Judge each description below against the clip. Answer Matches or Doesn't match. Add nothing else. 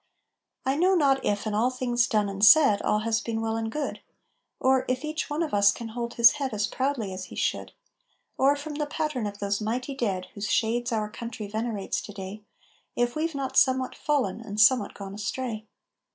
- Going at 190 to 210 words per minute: Matches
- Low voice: Doesn't match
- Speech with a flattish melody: Doesn't match